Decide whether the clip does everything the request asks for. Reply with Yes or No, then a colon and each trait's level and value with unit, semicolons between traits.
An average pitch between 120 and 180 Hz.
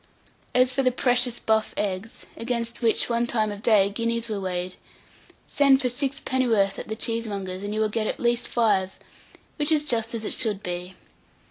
No: high, 225 Hz